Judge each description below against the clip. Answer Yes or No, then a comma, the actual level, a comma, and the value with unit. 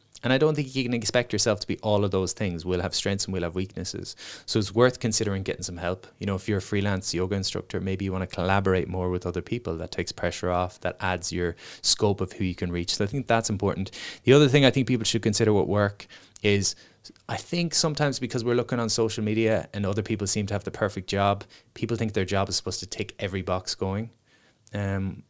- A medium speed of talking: No, fast, 245 wpm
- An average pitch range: Yes, average, 3.5 semitones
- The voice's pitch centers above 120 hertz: No, low, 100 Hz